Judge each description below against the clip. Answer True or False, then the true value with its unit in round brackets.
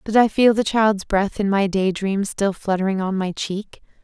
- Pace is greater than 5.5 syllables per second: False (4.6 syllables/s)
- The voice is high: True (200 Hz)